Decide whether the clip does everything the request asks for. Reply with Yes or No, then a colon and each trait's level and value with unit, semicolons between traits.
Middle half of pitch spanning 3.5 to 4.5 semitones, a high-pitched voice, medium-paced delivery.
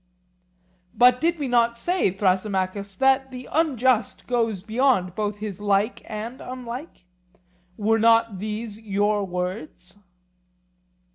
No: average, 3.9 semitones; high, 220 Hz; slow, 115 wpm